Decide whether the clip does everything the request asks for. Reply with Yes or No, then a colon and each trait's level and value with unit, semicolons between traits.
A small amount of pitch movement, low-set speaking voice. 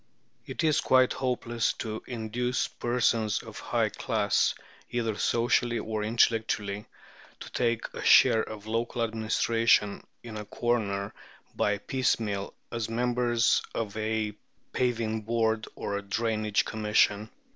Yes: narrow, 1.7 semitones; low, 110 Hz